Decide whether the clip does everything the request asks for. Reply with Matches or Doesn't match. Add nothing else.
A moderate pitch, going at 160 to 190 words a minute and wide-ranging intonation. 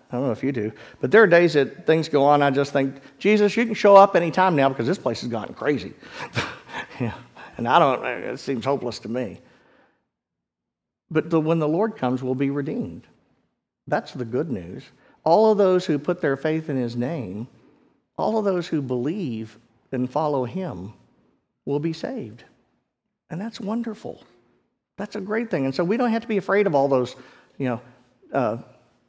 Doesn't match